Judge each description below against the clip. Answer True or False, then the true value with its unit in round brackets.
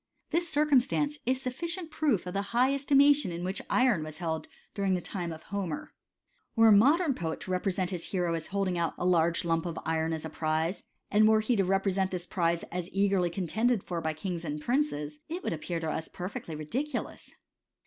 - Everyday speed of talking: False (210 wpm)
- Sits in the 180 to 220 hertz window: True (185 Hz)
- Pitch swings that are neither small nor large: False (6.6 semitones)